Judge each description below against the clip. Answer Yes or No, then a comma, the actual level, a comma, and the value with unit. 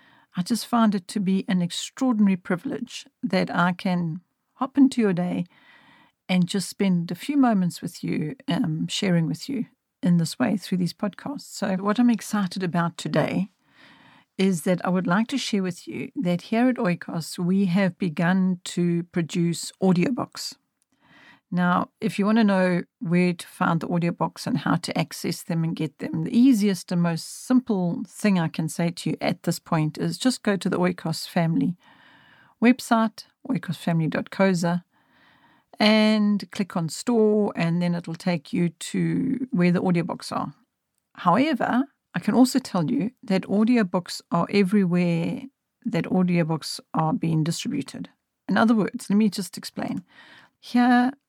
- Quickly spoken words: No, average, 160 wpm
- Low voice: No, high, 190 Hz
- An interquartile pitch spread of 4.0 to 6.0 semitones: Yes, average, 4.5 semitones